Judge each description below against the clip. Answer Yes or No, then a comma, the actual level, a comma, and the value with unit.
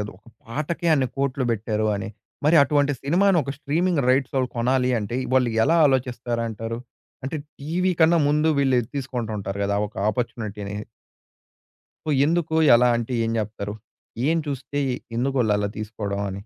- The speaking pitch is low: Yes, low, 125 Hz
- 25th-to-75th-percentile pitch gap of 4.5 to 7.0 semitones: Yes, average, 4.9 semitones